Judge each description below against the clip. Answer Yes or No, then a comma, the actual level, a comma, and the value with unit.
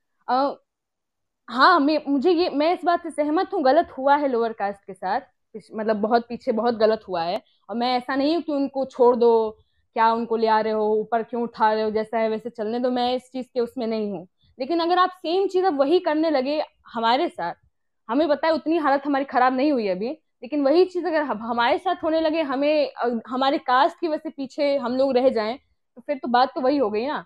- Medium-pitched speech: No, very high, 260 Hz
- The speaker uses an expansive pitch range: No, average, 4.9 semitones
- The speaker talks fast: Yes, fast, 235 wpm